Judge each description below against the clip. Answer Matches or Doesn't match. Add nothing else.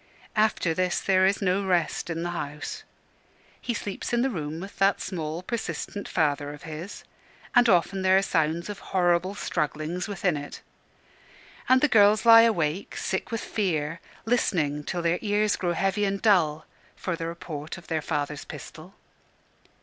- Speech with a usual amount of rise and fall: Matches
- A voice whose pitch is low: Doesn't match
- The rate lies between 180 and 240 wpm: Doesn't match